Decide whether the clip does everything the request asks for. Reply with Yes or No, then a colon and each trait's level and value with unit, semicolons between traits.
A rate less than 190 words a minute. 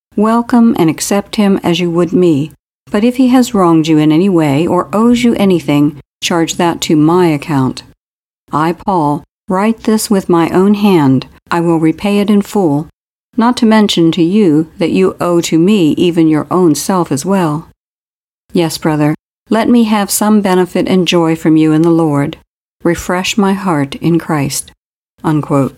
Yes: average, 175 wpm